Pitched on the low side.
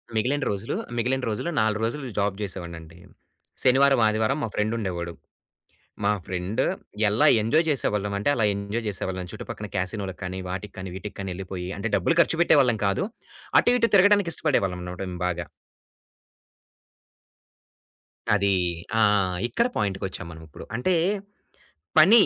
Yes: low, 105 Hz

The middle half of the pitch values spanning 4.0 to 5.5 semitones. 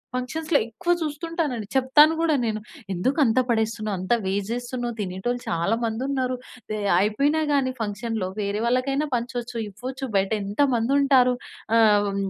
Yes: average, 4.3 semitones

